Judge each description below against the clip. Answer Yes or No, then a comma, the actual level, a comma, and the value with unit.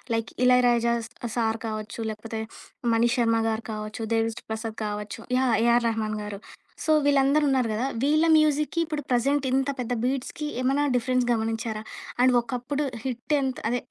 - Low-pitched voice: No, high, 240 Hz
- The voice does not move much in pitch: No, average, 3.0 semitones